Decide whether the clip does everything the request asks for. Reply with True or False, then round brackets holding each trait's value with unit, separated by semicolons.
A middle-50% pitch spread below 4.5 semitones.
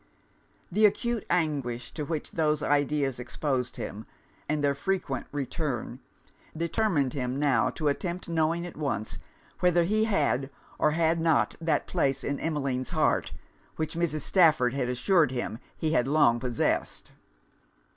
True (4.0 semitones)